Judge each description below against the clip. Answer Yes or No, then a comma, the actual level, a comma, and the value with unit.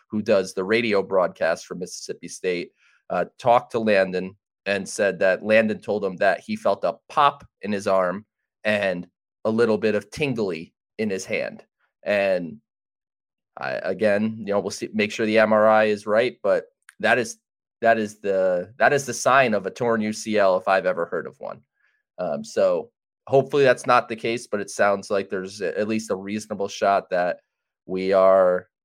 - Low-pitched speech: Yes, low, 105 Hz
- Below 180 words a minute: No, average, 185 wpm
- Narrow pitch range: Yes, narrow, 2.1 semitones